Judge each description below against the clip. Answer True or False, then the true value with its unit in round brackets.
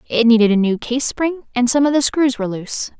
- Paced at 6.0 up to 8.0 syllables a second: True (6.1 syllables/s)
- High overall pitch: True (245 Hz)